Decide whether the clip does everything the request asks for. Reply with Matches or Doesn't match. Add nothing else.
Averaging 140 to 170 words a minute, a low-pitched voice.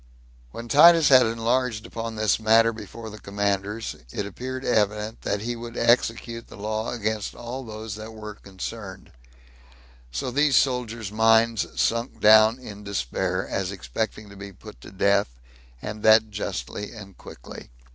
Matches